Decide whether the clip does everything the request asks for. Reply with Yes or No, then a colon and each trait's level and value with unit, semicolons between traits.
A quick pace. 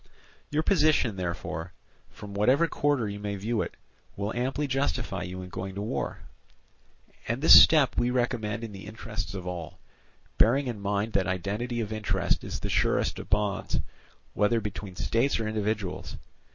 No: average, 165 wpm